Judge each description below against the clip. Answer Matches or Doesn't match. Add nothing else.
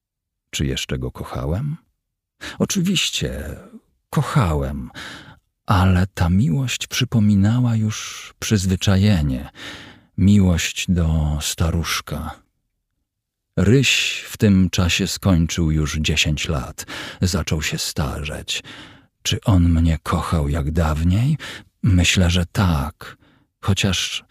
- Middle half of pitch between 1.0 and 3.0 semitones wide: Doesn't match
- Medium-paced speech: Doesn't match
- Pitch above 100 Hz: Doesn't match